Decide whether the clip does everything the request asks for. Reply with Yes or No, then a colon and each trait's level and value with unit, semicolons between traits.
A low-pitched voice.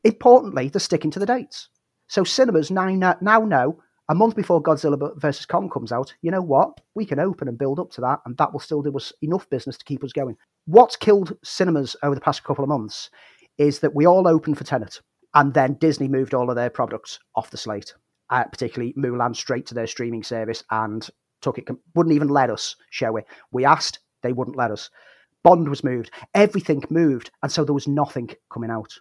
No: medium, 145 Hz